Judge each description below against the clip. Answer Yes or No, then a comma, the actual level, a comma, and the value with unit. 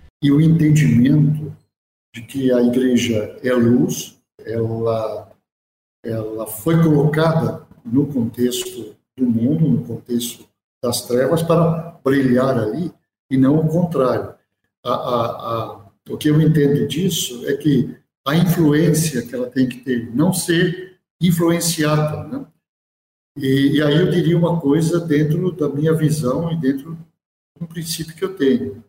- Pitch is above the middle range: No, medium, 145 Hz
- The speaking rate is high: No, average, 140 wpm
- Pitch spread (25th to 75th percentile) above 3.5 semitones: Yes, wide, 5.4 semitones